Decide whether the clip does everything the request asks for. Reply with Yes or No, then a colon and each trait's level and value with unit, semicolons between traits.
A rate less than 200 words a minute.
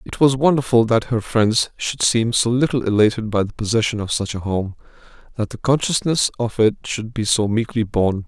No: fast, 205 wpm